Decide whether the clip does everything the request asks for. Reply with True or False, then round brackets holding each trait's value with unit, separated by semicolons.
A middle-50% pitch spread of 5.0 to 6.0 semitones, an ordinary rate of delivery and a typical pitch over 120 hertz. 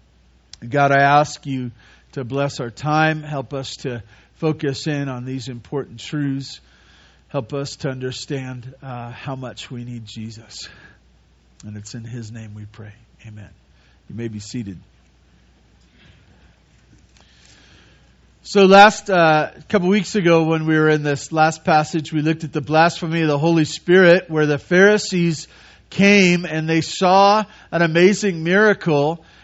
True (5.6 semitones; 145 wpm; 140 Hz)